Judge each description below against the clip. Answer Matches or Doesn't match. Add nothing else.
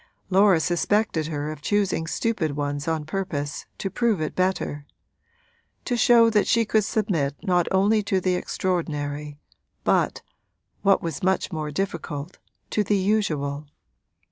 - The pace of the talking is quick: Doesn't match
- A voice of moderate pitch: Matches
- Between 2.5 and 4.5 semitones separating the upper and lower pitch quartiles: Doesn't match